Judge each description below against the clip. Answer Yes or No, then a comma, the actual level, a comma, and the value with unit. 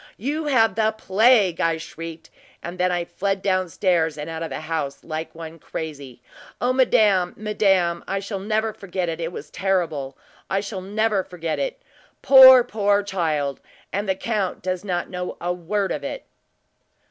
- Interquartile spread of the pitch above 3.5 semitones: Yes, average, 4.2 semitones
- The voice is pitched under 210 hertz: Yes, medium, 185 Hz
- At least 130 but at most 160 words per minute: No, average, 170 wpm